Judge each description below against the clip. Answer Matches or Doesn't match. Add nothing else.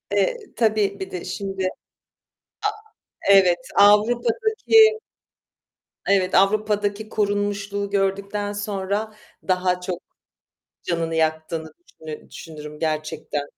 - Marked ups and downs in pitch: Doesn't match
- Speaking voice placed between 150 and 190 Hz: Doesn't match